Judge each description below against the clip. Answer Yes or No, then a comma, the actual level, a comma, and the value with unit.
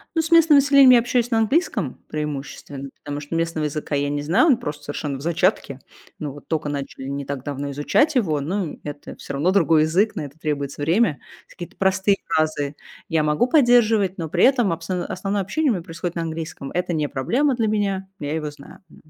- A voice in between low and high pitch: Yes, medium, 165 Hz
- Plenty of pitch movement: Yes, wide, 6.4 semitones